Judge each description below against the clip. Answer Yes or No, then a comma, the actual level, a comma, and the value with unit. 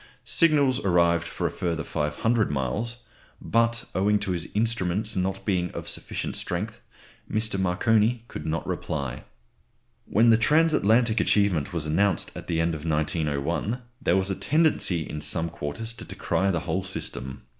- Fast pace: No, average, 155 wpm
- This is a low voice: Yes, very low, 95 Hz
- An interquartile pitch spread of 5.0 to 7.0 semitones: Yes, average, 5.3 semitones